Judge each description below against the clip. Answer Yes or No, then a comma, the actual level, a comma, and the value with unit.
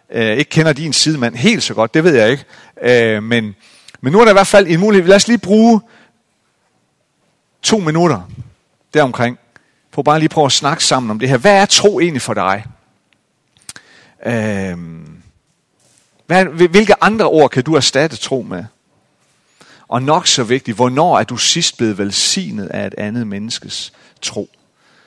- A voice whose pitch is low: No, medium, 150 Hz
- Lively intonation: Yes, wide, 8.2 semitones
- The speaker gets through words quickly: No, average, 160 wpm